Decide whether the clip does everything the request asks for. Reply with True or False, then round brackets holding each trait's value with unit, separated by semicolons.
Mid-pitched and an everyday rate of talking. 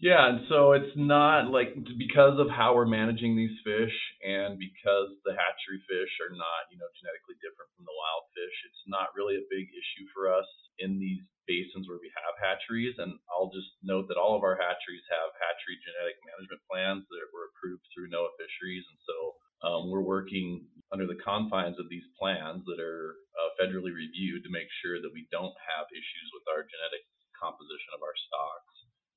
False (110 Hz; 195 wpm)